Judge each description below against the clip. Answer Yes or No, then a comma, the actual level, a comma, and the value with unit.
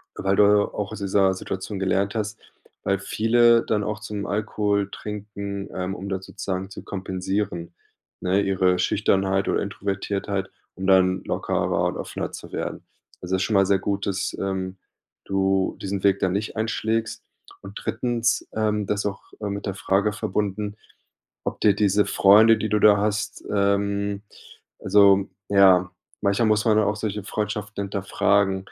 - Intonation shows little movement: Yes, narrow, 1.5 semitones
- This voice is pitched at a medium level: No, low, 100 Hz